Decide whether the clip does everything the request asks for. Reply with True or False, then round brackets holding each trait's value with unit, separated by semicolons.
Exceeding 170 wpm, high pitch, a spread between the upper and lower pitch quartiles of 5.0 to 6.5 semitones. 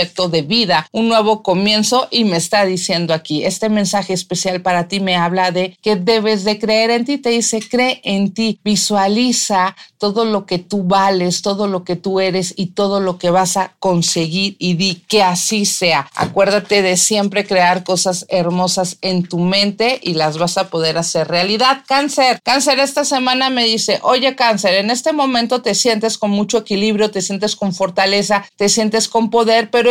False (185 wpm; 200 Hz; 3.4 semitones)